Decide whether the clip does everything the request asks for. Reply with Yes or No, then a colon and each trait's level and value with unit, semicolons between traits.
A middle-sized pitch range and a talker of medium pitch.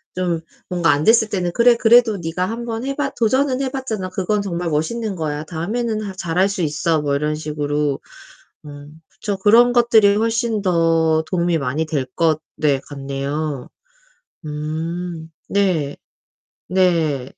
No: wide, 5.9 semitones; medium, 175 Hz